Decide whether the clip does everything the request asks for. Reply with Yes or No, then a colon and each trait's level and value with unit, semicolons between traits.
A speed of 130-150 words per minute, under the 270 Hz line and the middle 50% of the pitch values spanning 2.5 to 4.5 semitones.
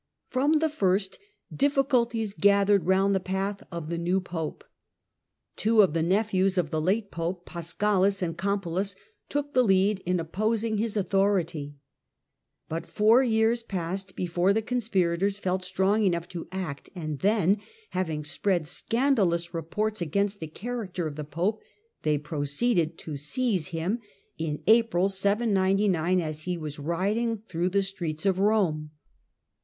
Yes: average, 145 wpm; high, 190 Hz; average, 3.9 semitones